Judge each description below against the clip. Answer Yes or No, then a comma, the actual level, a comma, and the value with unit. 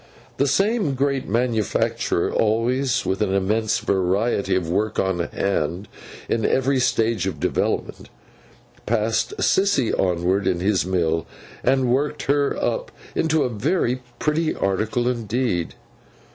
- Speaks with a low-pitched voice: Yes, low, 115 Hz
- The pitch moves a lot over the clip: Yes, wide, 5.7 semitones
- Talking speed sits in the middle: No, slow, 125 wpm